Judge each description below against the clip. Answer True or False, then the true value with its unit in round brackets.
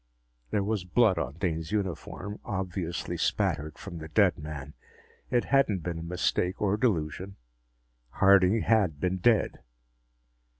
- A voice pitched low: True (90 Hz)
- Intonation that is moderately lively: True (3.9 semitones)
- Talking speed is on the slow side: True (130 wpm)